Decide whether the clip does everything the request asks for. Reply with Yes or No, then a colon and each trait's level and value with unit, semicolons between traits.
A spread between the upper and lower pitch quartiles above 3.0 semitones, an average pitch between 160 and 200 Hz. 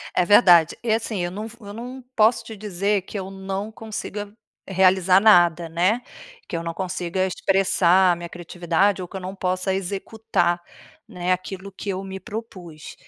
No: average, 2.7 semitones; high, 190 Hz